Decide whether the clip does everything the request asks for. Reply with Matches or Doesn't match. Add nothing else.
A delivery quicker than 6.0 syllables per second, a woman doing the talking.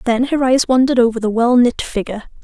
Matches